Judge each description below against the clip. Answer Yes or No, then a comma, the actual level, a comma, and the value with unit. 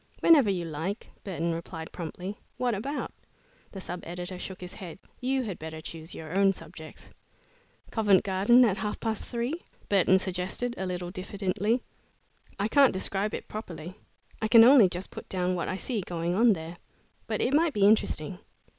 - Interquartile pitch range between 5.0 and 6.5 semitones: No, average, 4.0 semitones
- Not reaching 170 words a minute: No, average, 175 wpm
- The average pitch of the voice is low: No, high, 190 Hz